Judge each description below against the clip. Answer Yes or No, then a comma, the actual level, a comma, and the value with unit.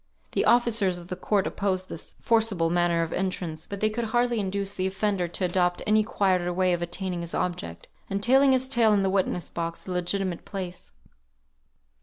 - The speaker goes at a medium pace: Yes, average, 190 wpm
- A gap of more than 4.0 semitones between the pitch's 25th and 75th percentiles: No, average, 3.2 semitones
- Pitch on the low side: No, high, 190 Hz